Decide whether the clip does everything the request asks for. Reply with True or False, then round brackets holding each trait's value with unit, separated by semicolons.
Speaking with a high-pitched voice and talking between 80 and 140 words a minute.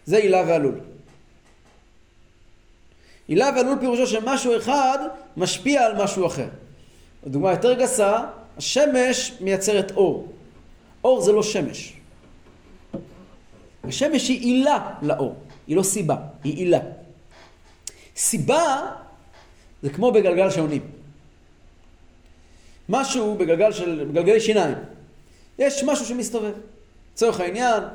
True (205 Hz; 100 wpm)